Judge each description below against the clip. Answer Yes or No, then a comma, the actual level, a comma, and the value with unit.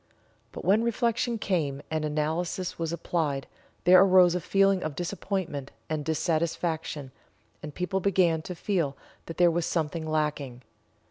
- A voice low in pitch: No, medium, 165 Hz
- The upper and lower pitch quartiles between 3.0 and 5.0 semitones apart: Yes, average, 3.3 semitones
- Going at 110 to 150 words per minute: Yes, average, 140 wpm